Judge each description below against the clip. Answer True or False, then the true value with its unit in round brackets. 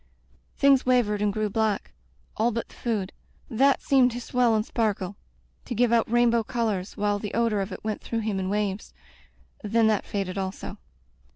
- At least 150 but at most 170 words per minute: False (190 wpm)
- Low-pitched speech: False (220 Hz)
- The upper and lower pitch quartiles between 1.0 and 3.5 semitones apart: True (2.5 semitones)